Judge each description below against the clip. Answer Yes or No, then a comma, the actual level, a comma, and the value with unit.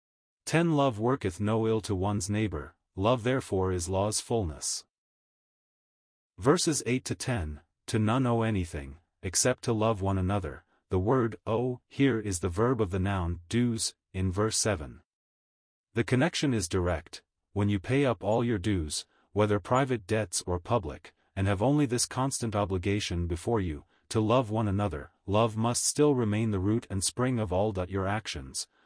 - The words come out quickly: No, average, 165 wpm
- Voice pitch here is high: No, low, 105 Hz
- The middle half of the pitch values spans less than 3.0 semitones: No, average, 4.4 semitones